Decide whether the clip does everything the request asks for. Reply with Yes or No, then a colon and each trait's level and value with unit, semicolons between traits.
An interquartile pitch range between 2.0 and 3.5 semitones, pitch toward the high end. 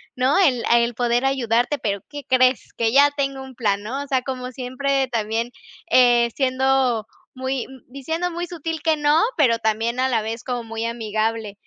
Yes: average, 2.9 semitones; very high, 255 Hz